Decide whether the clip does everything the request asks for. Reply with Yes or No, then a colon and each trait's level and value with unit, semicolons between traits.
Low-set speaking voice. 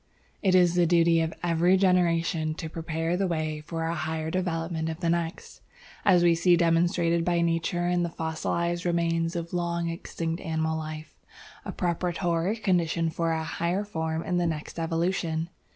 No: medium, 170 Hz